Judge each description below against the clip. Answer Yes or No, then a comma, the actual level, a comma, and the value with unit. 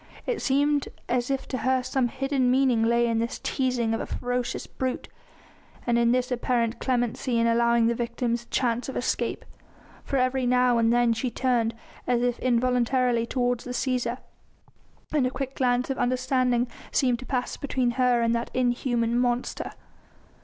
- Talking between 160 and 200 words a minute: Yes, average, 170 wpm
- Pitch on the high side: Yes, high, 245 Hz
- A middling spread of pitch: No, narrow, 1.4 semitones